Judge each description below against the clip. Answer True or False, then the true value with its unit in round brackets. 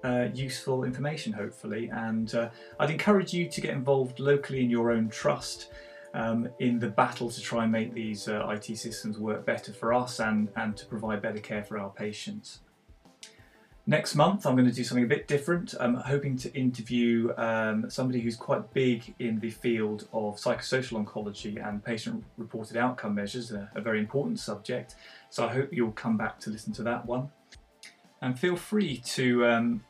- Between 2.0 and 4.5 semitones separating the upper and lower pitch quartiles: True (3.0 semitones)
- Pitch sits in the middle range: False (120 Hz)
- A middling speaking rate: True (185 wpm)